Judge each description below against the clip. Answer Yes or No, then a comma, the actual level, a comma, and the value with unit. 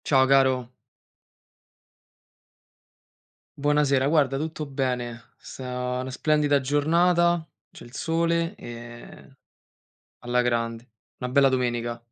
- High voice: No, low, 135 Hz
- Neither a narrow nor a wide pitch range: Yes, average, 3.2 semitones